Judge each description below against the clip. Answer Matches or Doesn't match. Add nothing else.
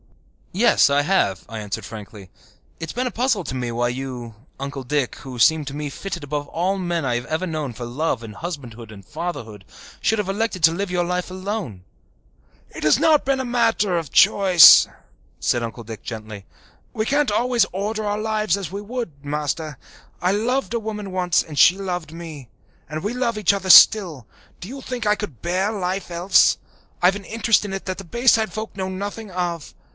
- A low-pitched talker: Doesn't match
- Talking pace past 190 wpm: Matches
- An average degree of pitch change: Doesn't match